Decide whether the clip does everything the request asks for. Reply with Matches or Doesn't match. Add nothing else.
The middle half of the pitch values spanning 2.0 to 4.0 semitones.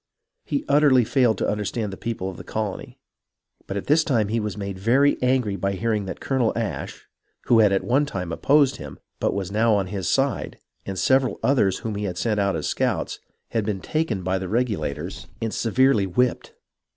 Doesn't match